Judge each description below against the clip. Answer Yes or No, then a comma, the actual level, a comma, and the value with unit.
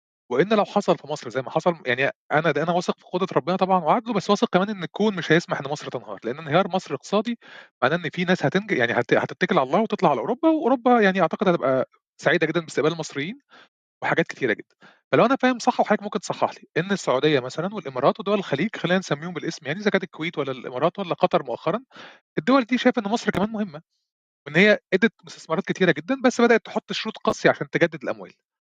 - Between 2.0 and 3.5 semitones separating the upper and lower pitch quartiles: No, wide, 5.4 semitones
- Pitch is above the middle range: No, medium, 180 Hz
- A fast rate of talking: Yes, fast, 215 wpm